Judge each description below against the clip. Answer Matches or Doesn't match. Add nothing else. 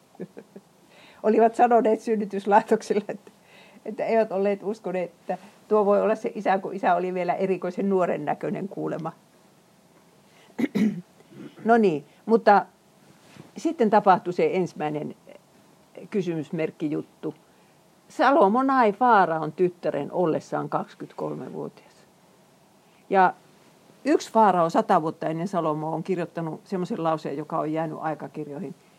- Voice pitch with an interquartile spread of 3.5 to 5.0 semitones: Matches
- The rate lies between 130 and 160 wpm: Doesn't match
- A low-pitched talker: Doesn't match